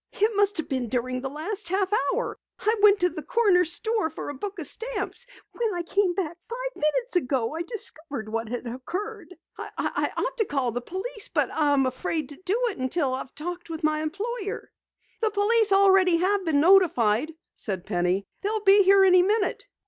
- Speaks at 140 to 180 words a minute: No, average, 195 wpm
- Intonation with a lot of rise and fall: Yes, wide, 6.4 semitones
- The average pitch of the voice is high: Yes, very high, 360 Hz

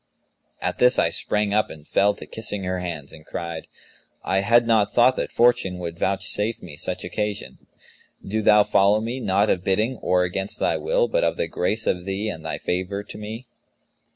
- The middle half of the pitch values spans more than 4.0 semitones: No, average, 3.3 semitones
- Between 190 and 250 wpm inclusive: Yes, average, 195 wpm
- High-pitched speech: No, low, 100 Hz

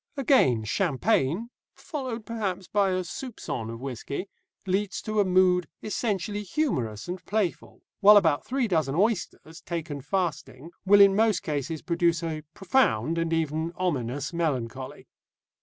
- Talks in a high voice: No, medium, 175 Hz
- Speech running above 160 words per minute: No, slow, 135 wpm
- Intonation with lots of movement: Yes, wide, 5.7 semitones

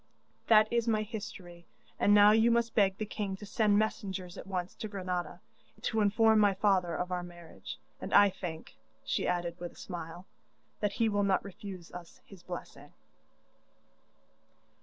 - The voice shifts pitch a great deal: No, average, 3.1 semitones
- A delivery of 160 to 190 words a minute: Yes, average, 165 wpm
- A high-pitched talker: Yes, high, 195 Hz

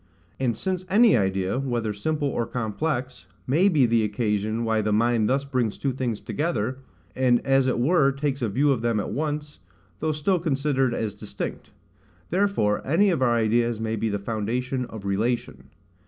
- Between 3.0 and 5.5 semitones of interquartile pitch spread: Yes, average, 4.4 semitones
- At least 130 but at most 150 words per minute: No, average, 175 wpm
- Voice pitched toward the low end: Yes, low, 125 Hz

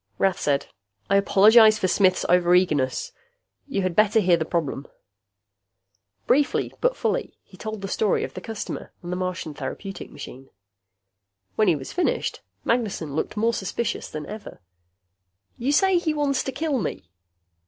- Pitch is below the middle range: No, high, 195 Hz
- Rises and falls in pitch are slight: No, average, 5.0 semitones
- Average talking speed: Yes, average, 155 wpm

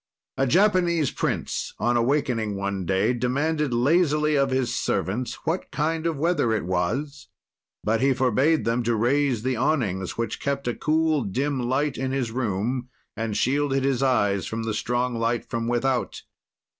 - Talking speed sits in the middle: Yes, average, 160 wpm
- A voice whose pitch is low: Yes, low, 130 Hz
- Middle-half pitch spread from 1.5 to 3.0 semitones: No, average, 4.0 semitones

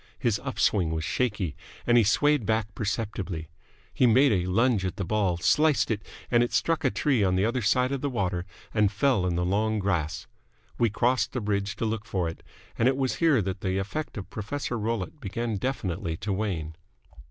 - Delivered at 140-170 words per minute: No, fast, 205 wpm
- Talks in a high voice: No, low, 105 Hz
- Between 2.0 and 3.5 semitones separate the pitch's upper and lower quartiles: No, average, 4.5 semitones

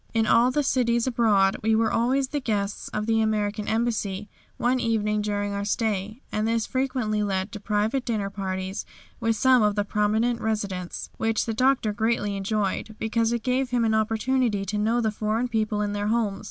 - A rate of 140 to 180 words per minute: No, average, 190 wpm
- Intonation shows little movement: Yes, narrow, 2.2 semitones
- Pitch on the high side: Yes, high, 220 Hz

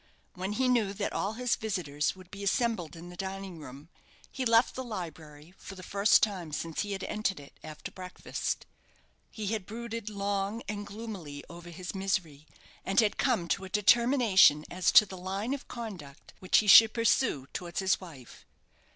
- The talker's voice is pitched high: Yes, high, 195 Hz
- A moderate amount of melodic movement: Yes, average, 4.0 semitones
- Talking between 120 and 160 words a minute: No, average, 180 wpm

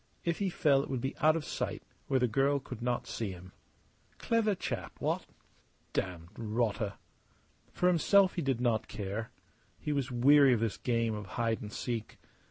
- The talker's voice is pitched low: Yes, low, 125 Hz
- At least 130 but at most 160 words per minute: No, average, 180 wpm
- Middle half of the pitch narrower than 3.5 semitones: No, average, 4.8 semitones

